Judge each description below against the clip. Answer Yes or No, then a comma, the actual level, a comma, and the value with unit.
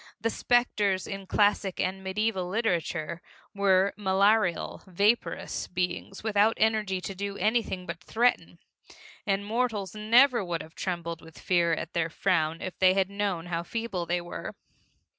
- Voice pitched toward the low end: No, high, 195 Hz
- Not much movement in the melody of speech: No, average, 3.2 semitones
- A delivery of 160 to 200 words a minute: No, average, 145 wpm